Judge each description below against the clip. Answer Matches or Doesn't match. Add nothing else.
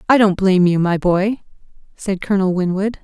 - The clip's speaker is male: Doesn't match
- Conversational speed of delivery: Matches